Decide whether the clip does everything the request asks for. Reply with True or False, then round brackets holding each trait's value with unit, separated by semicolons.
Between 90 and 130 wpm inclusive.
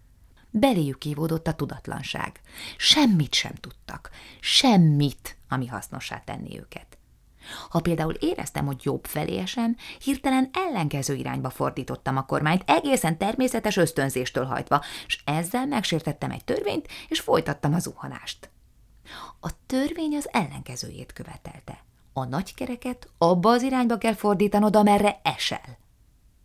True (120 wpm)